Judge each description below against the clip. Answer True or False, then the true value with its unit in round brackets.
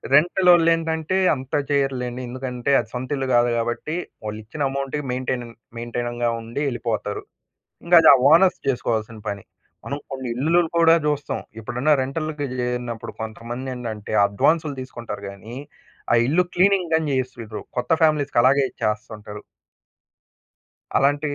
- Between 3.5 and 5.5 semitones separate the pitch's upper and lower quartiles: True (4.2 semitones)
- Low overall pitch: True (130 Hz)